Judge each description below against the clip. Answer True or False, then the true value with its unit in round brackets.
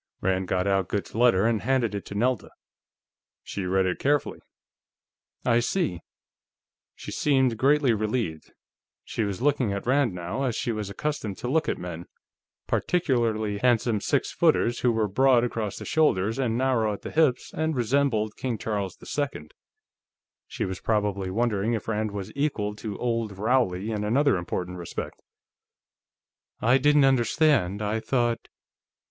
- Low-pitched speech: True (115 Hz)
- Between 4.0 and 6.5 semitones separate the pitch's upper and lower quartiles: True (4.5 semitones)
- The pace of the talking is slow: False (155 wpm)